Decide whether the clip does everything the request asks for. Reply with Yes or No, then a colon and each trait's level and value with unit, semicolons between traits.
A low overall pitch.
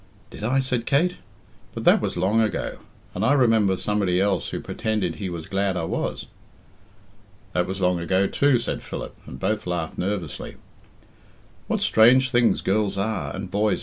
Yes: low, 100 Hz